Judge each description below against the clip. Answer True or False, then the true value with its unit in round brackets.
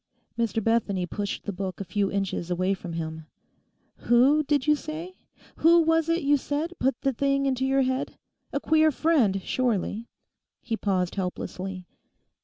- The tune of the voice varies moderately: False (7.1 semitones)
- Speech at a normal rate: True (155 wpm)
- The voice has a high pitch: True (235 Hz)